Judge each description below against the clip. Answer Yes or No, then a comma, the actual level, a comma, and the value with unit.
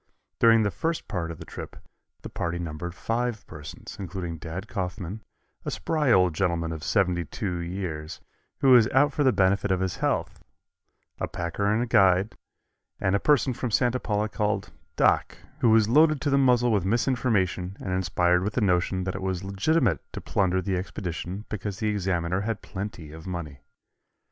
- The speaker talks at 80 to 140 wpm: No, average, 180 wpm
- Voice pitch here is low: Yes, very low, 95 Hz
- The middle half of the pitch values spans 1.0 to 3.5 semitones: No, average, 4.3 semitones